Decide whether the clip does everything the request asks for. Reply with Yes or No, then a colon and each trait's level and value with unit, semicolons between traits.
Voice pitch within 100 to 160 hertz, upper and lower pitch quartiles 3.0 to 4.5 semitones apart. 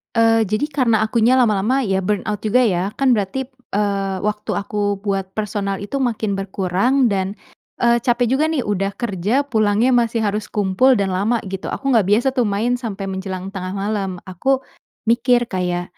No: high, 210 Hz; average, 3.7 semitones